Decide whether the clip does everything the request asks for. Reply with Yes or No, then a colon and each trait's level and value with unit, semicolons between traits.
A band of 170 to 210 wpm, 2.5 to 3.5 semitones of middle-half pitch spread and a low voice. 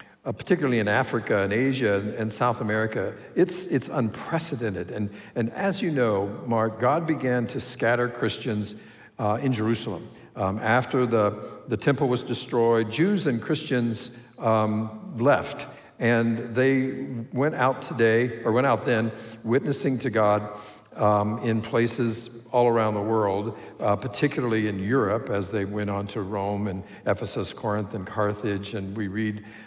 No: average, 150 wpm; average, 3.0 semitones; low, 115 Hz